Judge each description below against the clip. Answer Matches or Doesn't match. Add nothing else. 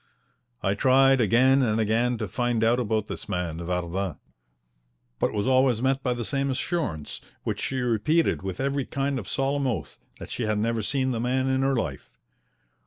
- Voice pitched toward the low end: Matches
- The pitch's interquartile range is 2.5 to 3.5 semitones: Doesn't match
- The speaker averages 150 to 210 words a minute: Matches